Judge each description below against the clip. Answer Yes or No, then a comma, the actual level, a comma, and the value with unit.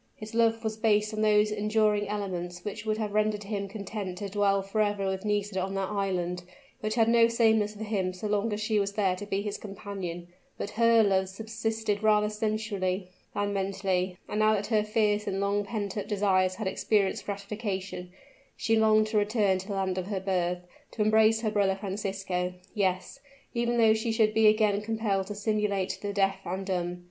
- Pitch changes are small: Yes, narrow, 1.9 semitones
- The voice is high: Yes, high, 205 Hz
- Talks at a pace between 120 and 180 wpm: No, average, 195 wpm